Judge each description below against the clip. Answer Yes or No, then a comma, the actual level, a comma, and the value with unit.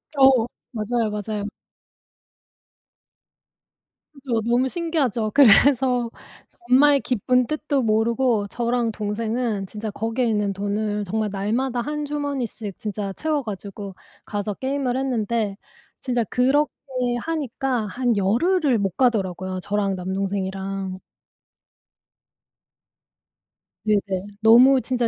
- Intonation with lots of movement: No, average, 4.2 semitones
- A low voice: No, high, 225 Hz